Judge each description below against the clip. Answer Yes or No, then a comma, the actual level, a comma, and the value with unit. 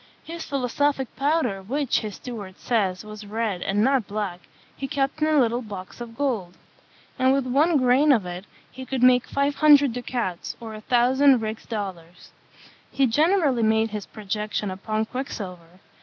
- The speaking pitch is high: Yes, high, 235 Hz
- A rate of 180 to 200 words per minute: No, average, 165 wpm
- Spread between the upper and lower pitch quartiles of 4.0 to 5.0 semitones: Yes, average, 4.7 semitones